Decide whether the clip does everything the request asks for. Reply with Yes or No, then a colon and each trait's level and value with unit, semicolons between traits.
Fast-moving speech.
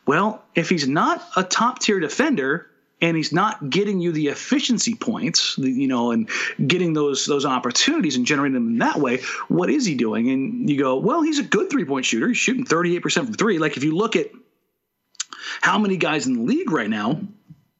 Yes: fast, 210 wpm